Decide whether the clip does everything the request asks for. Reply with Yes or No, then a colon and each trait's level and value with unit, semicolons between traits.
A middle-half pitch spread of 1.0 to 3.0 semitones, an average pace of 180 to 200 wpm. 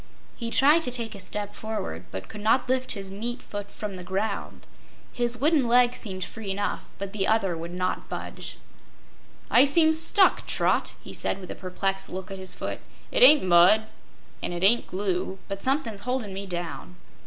No: average, 4.4 semitones; average, 190 wpm